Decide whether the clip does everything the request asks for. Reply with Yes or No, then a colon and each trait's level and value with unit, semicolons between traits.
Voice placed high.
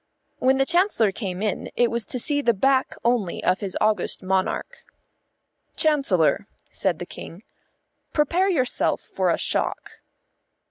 Yes: high, 235 Hz